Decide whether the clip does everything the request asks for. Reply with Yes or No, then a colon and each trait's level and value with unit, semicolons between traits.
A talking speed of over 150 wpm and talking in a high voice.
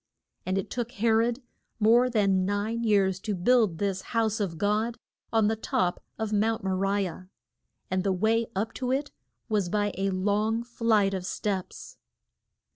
Yes: average, 170 wpm; high, 210 Hz